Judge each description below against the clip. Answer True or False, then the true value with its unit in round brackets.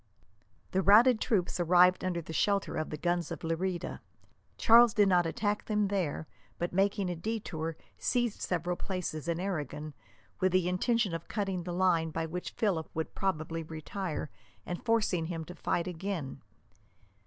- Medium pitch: True (180 Hz)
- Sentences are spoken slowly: False (160 wpm)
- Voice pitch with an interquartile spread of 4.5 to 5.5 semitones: False (3.3 semitones)